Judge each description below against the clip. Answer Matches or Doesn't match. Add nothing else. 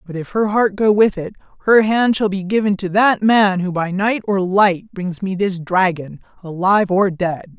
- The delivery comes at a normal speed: Doesn't match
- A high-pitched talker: Matches